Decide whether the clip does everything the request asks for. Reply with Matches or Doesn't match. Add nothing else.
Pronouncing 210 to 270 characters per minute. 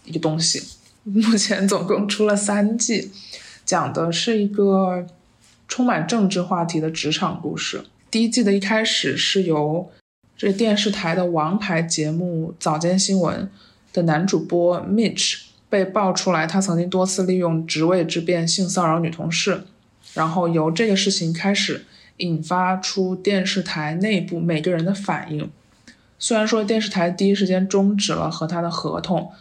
Matches